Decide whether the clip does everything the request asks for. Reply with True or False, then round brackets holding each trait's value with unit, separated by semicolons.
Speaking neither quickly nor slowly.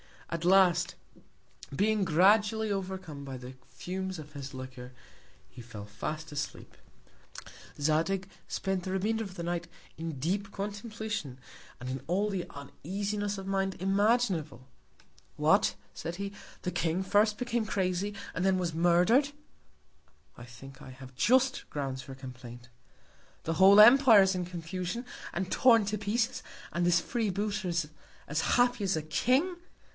True (145 wpm)